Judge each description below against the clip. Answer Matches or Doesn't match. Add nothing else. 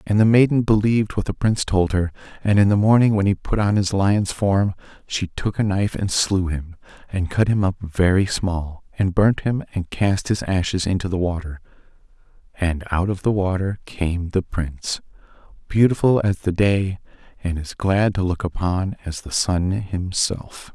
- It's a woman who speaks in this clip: Doesn't match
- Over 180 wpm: Matches